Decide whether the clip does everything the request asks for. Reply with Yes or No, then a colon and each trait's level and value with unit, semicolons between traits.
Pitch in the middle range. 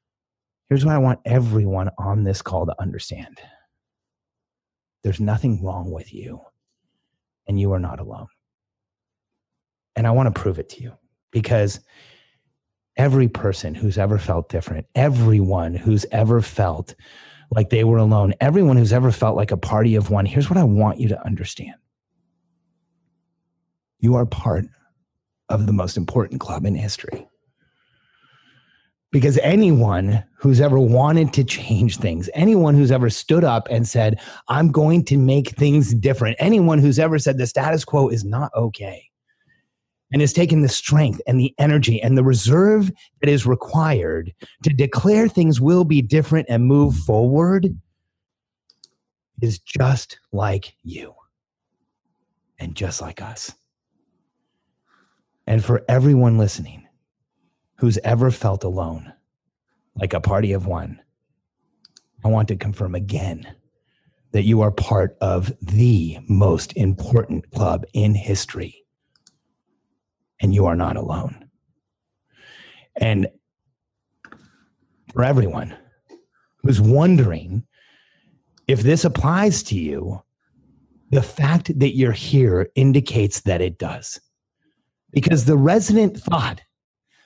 No: low, 115 Hz